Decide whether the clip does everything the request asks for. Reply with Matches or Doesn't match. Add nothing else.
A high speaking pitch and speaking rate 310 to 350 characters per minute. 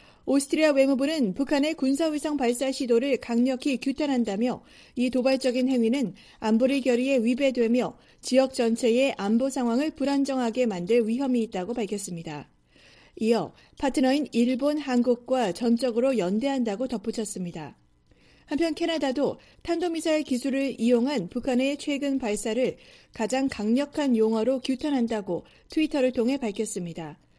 Matches